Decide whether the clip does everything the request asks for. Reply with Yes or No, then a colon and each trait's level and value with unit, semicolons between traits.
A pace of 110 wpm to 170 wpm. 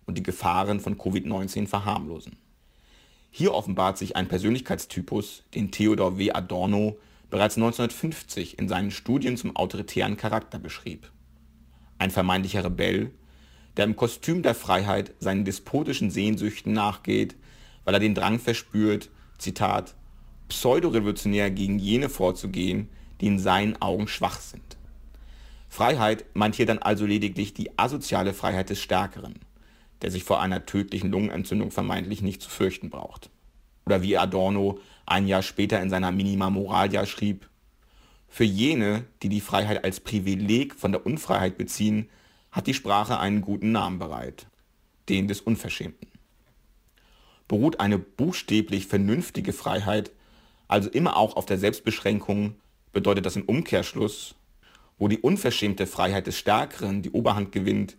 Yes: average, 135 wpm